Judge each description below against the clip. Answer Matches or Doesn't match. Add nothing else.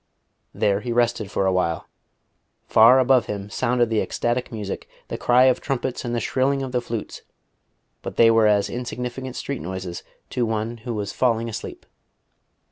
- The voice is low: Matches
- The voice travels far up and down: Doesn't match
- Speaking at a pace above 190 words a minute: Doesn't match